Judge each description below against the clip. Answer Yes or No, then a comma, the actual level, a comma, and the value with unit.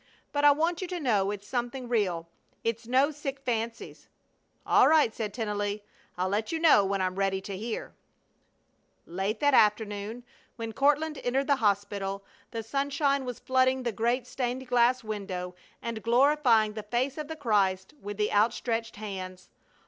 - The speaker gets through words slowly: No, average, 165 wpm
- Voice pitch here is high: Yes, high, 230 Hz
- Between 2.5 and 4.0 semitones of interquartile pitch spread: No, average, 4.5 semitones